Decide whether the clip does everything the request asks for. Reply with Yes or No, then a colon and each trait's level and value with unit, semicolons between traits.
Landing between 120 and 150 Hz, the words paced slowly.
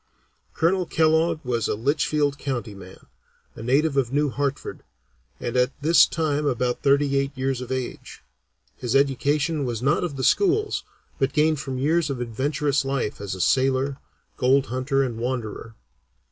No: low, 135 Hz; average, 155 wpm